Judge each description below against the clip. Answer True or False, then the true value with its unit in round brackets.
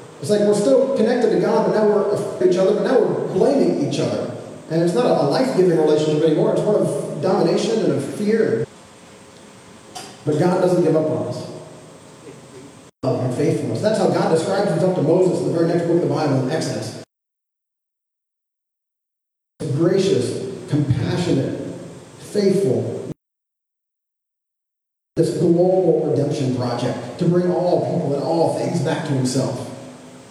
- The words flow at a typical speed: True (150 wpm)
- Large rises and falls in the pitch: False (4.4 semitones)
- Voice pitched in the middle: True (165 Hz)